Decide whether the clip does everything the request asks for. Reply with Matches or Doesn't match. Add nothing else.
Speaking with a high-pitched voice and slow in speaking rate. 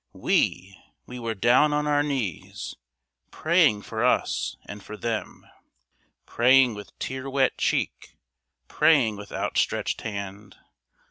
Doesn't match